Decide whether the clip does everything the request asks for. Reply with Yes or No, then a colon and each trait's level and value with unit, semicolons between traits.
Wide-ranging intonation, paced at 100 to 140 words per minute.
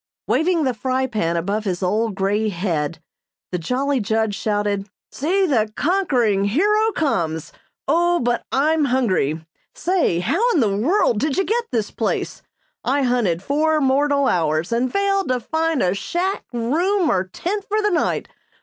No: wide, 8.3 semitones; average, 160 wpm